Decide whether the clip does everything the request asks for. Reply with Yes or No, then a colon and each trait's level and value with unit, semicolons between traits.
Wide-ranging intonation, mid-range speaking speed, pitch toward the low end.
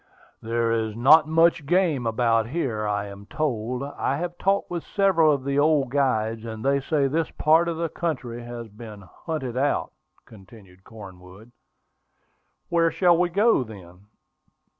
Yes: wide, 6.4 semitones; average, 155 wpm; low, 130 Hz